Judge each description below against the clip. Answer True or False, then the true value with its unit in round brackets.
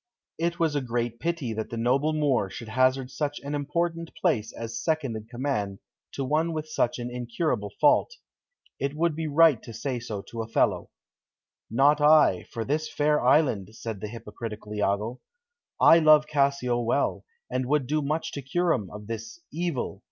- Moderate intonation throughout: True (5.0 semitones)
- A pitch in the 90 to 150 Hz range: True (135 Hz)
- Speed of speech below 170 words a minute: False (175 wpm)